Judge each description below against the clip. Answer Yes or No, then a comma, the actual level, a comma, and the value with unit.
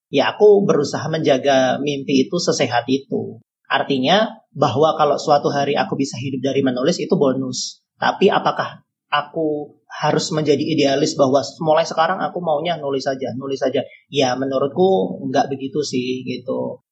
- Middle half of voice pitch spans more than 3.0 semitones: No, narrow, 2.4 semitones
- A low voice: No, medium, 145 Hz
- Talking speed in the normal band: No, fast, 145 wpm